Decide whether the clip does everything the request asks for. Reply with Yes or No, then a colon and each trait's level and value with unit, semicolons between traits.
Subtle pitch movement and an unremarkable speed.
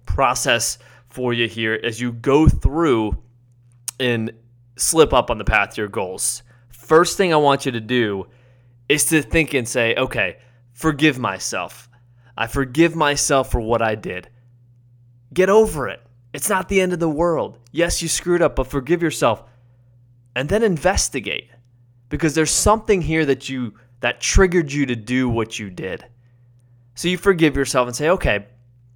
No: average, 4.3 semitones; average, 165 wpm